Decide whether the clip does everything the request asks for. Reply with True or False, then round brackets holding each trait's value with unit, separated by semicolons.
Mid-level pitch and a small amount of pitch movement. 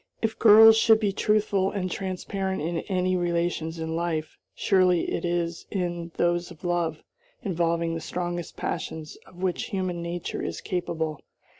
True (175 Hz; 2.1 semitones)